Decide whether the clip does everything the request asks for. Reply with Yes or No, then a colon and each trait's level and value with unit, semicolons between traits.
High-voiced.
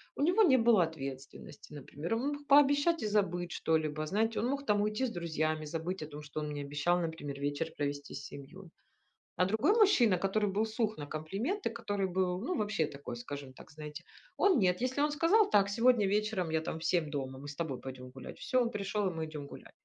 No: medium, 180 Hz